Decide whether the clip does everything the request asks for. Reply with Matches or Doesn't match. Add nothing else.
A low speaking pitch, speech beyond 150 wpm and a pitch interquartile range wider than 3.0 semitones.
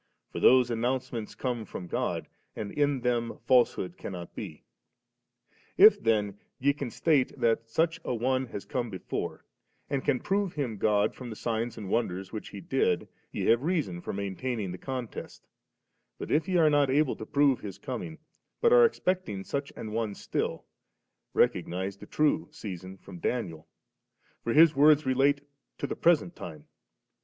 Matches